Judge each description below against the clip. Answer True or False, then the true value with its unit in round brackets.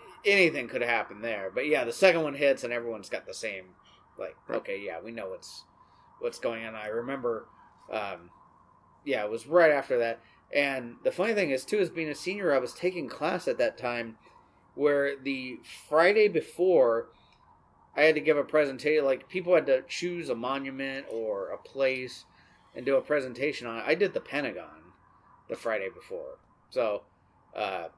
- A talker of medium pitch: True (170 Hz)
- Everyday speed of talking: True (180 wpm)